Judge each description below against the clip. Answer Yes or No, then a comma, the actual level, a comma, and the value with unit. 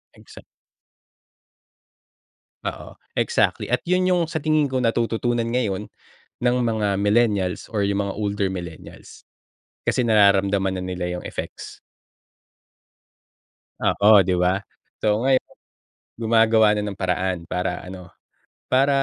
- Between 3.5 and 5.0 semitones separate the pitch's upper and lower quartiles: Yes, average, 3.8 semitones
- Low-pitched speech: Yes, low, 105 Hz